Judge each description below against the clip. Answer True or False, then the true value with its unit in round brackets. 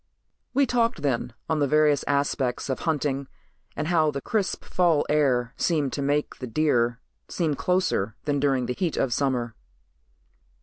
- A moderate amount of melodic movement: True (3.4 semitones)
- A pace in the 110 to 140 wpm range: False (160 wpm)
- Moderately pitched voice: True (145 Hz)